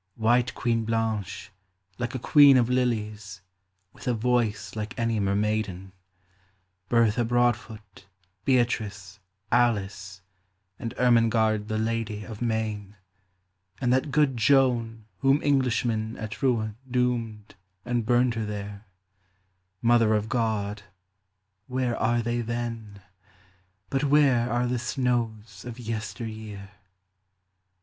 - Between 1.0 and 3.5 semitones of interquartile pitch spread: Yes, narrow, 2.6 semitones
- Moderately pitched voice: No, low, 115 Hz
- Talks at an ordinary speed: No, slow, 120 wpm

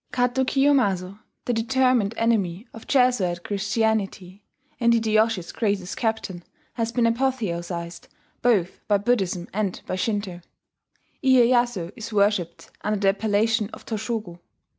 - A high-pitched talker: Yes, high, 215 Hz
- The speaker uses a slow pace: Yes, slow, 120 wpm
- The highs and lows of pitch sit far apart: No, average, 3.6 semitones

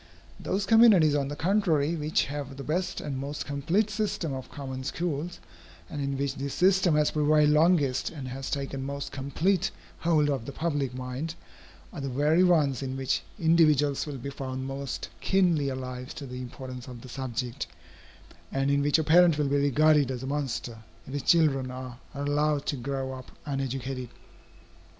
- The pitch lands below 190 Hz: Yes, medium, 140 Hz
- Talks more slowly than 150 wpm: No, average, 175 wpm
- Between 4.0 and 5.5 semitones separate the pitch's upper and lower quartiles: No, average, 2.7 semitones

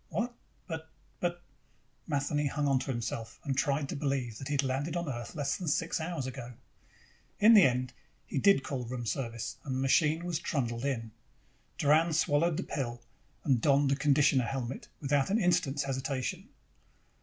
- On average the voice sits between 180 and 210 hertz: No, medium, 140 Hz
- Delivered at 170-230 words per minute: Yes, average, 175 wpm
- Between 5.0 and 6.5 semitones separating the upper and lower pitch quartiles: No, average, 3.4 semitones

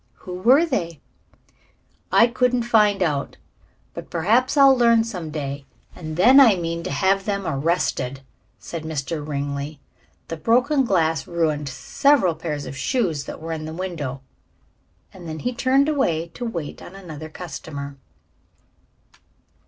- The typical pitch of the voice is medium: Yes, medium, 170 Hz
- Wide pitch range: Yes, wide, 6.9 semitones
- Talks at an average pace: Yes, average, 145 wpm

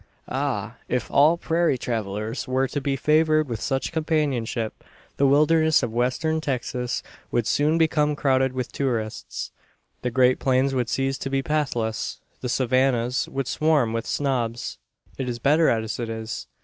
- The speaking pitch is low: Yes, low, 130 Hz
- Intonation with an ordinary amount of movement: Yes, average, 3.8 semitones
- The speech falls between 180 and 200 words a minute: No, average, 155 wpm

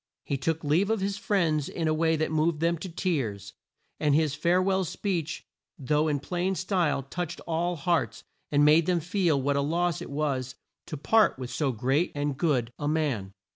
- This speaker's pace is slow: No, average, 195 wpm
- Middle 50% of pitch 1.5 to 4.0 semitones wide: Yes, average, 3.6 semitones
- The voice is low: No, medium, 155 Hz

